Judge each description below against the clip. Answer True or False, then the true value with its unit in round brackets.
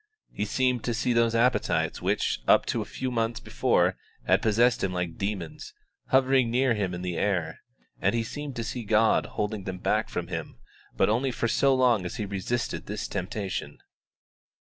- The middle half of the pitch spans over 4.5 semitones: False (4.0 semitones)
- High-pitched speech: False (115 Hz)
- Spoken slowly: False (185 wpm)